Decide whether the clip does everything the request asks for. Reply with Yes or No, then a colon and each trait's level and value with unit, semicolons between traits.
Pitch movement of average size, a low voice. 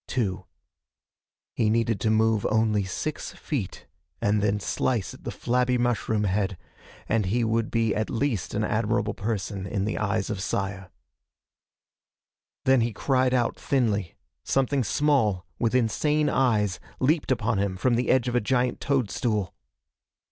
Yes: average, 3.5 semitones; low, 110 Hz